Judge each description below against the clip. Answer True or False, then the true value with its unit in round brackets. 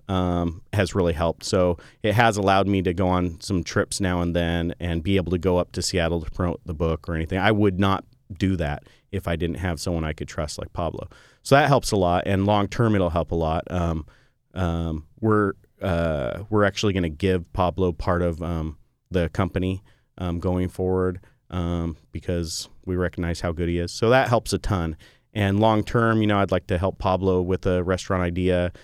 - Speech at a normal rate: False (215 wpm)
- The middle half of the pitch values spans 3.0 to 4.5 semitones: False (2.5 semitones)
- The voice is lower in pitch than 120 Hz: True (90 Hz)